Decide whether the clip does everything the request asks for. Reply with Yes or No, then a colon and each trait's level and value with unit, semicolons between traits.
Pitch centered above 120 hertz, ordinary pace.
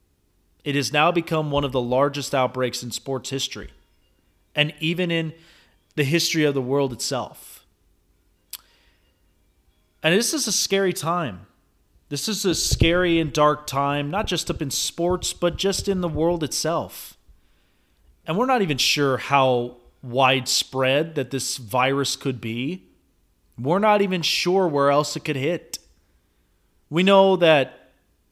Yes: low, 135 Hz; average, 145 wpm